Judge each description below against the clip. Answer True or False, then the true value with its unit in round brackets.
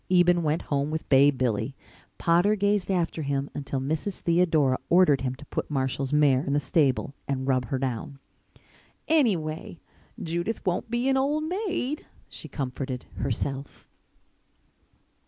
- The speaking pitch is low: False (150 Hz)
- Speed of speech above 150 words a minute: False (140 wpm)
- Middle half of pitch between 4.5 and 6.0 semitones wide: True (5.1 semitones)